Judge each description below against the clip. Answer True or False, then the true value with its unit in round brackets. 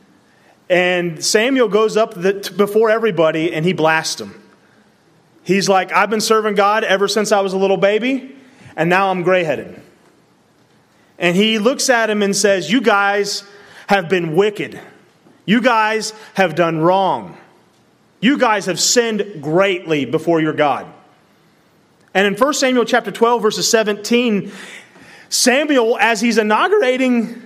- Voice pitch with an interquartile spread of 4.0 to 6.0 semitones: False (3.5 semitones)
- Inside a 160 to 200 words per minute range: False (140 wpm)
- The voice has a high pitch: True (205 Hz)